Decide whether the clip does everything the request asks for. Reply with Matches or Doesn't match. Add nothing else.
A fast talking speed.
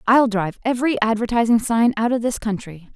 Doesn't match